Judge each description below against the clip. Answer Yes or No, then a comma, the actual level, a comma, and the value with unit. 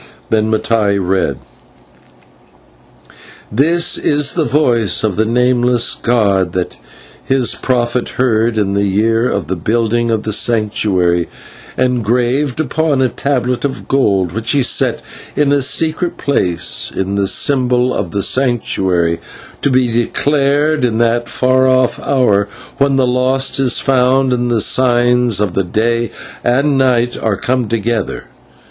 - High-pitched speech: No, low, 120 Hz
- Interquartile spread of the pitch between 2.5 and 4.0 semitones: Yes, average, 3.5 semitones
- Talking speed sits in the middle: Yes, average, 145 wpm